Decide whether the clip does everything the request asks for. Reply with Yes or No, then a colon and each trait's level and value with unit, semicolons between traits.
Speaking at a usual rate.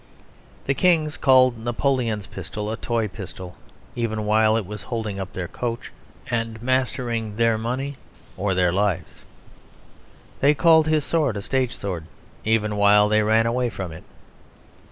Yes: average, 150 wpm